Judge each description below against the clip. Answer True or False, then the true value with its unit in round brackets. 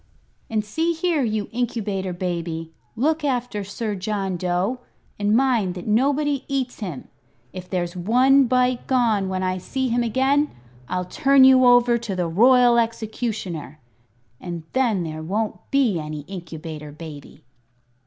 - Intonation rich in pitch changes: True (5.8 semitones)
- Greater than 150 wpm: False (145 wpm)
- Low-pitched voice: False (215 Hz)